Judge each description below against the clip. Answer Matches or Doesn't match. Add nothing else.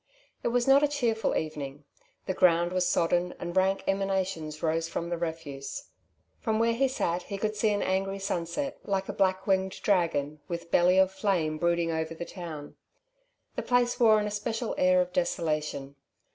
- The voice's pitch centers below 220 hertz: Matches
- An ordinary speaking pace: Matches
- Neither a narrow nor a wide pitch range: Matches